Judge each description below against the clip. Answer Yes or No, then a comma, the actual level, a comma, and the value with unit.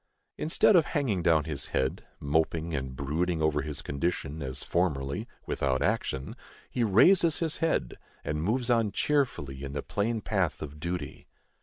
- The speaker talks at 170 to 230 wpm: No, average, 155 wpm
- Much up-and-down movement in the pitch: Yes, wide, 7.9 semitones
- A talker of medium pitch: No, very low, 80 Hz